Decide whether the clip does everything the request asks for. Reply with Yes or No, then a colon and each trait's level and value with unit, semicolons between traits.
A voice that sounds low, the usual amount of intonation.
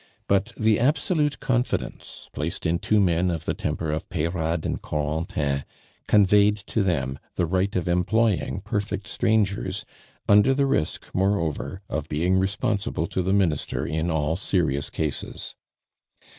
Yes: very low, 95 Hz; average, 4.4 semitones